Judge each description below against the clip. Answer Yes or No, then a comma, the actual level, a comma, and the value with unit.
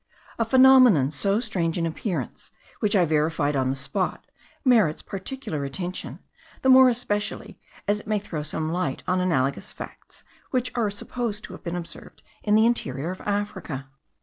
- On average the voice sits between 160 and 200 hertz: Yes, medium, 185 Hz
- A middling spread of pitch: No, wide, 5.9 semitones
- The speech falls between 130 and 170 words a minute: Yes, average, 165 wpm